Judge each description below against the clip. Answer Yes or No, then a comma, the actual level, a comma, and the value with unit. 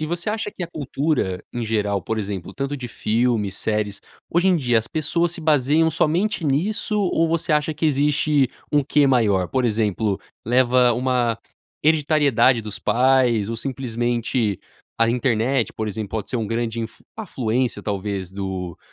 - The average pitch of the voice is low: Yes, low, 125 Hz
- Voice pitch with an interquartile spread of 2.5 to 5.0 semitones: No, wide, 5.4 semitones